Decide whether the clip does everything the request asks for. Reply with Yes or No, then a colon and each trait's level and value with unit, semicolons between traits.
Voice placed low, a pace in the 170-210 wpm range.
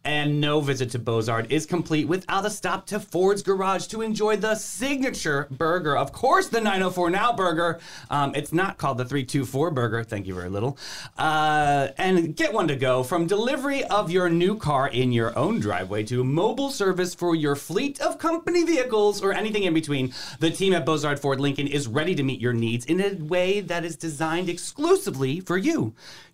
No: medium, 165 Hz; average, 195 wpm